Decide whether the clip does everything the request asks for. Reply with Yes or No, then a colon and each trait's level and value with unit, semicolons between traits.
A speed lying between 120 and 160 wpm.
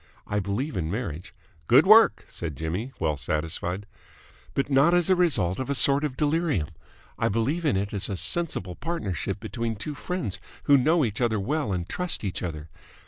No: average, 195 wpm